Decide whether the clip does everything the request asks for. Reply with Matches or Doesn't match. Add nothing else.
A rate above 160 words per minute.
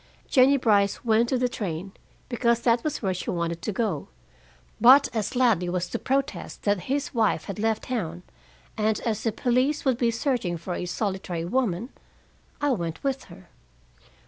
Matches